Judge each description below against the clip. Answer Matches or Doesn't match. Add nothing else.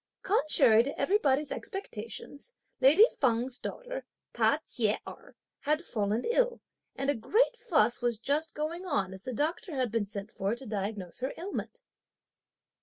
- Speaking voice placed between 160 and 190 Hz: Doesn't match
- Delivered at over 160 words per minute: Doesn't match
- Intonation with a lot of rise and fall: Matches